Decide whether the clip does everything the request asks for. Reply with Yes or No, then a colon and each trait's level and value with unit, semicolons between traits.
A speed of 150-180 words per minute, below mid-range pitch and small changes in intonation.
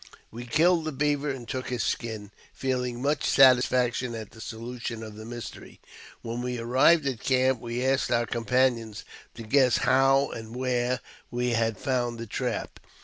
Yes: average, 170 wpm; low, 125 Hz; narrow, 2.1 semitones